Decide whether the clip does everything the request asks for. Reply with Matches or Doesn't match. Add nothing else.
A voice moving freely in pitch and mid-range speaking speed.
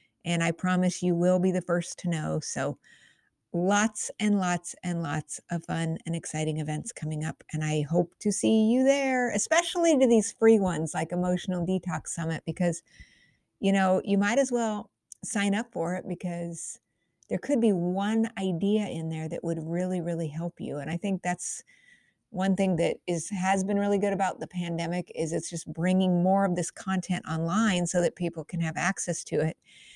Doesn't match